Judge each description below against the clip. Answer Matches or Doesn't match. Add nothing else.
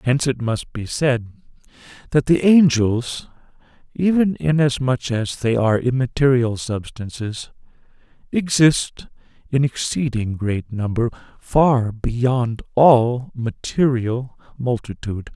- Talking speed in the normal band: Doesn't match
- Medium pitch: Doesn't match